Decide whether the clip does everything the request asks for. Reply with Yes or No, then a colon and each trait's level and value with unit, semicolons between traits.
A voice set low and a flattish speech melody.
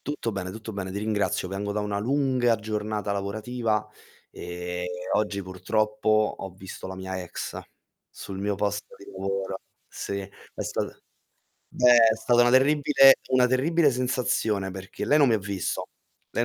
No: low, 105 Hz; average, 3.9 semitones